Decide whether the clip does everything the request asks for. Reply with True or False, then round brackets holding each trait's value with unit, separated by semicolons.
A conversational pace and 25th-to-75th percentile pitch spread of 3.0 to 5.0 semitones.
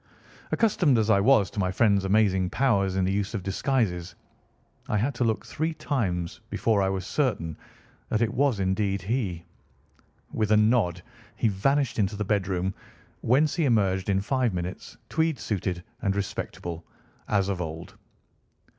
True (160 wpm; 4.2 semitones)